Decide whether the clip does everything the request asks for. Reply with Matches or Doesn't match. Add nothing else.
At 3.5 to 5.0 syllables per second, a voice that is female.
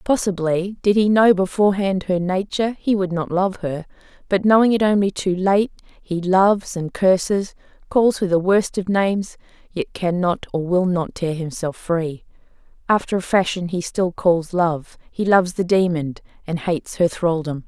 Matches